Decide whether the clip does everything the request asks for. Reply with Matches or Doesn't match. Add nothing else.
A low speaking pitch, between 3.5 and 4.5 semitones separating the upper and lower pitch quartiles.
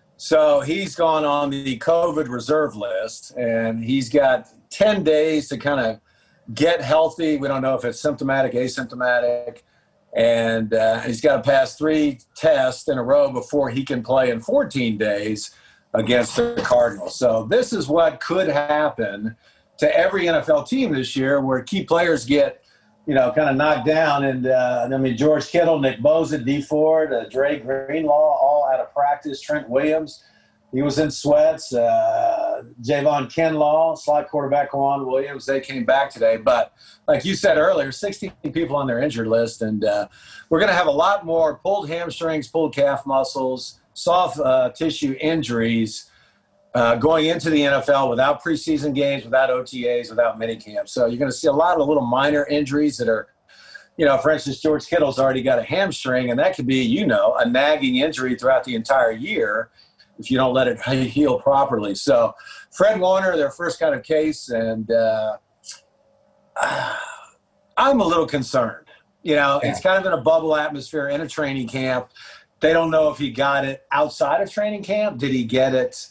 Doesn't match